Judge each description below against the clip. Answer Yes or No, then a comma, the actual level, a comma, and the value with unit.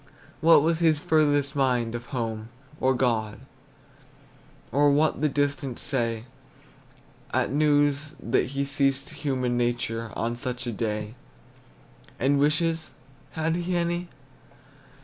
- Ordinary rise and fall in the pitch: Yes, average, 4.1 semitones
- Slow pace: Yes, slow, 120 wpm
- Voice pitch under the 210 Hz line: Yes, medium, 140 Hz